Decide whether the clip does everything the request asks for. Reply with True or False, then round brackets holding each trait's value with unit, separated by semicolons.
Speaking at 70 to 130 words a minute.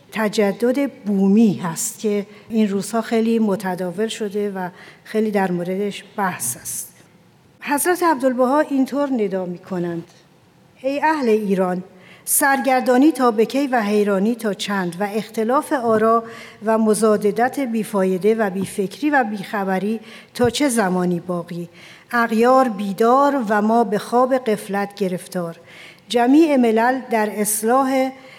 True (120 wpm)